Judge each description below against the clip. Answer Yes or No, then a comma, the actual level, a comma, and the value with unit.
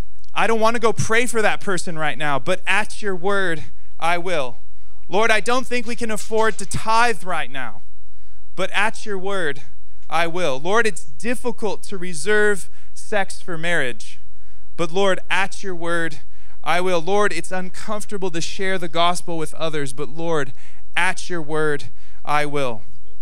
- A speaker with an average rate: Yes, average, 170 wpm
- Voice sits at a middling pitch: Yes, medium, 170 Hz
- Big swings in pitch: Yes, wide, 7.5 semitones